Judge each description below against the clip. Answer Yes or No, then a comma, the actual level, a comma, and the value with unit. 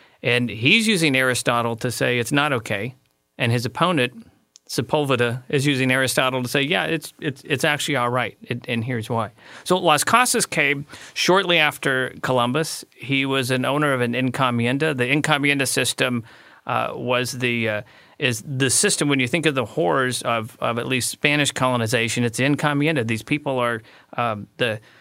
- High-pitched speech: No, low, 130 Hz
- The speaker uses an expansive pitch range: No, average, 3.2 semitones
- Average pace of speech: Yes, average, 175 wpm